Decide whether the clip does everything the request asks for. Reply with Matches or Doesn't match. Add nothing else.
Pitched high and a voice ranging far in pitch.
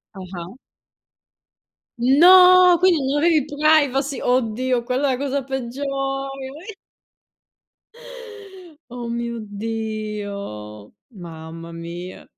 Matches